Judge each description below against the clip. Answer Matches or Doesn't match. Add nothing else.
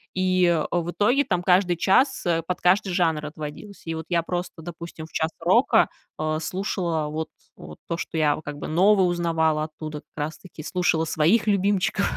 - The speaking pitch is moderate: Matches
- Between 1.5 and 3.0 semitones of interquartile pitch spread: Matches